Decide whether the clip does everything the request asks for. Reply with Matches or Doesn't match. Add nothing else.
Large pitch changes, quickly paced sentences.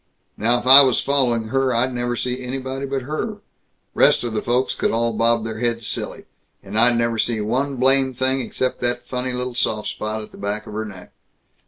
Doesn't match